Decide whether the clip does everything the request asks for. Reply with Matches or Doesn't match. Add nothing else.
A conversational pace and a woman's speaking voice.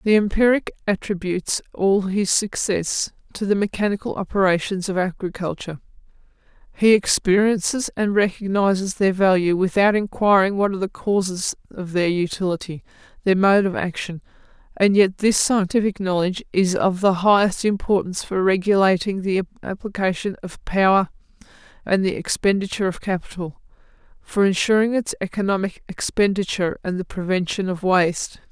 Doesn't match